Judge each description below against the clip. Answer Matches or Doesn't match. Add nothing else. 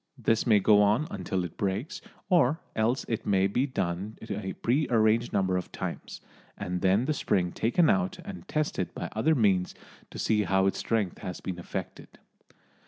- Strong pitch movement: Doesn't match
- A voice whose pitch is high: Doesn't match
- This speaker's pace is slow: Doesn't match